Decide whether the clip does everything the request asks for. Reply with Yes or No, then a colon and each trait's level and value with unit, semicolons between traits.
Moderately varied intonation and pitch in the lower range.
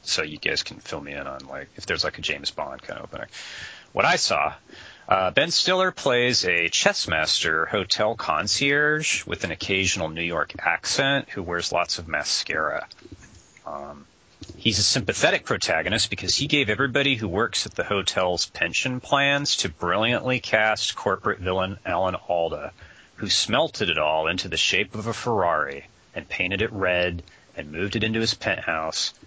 No: wide, 6.6 semitones; low, 100 Hz